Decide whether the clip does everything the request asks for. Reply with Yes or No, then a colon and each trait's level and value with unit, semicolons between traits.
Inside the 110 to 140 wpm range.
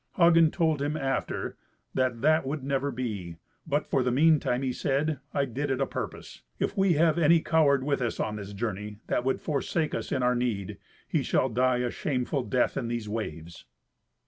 No: average, 195 wpm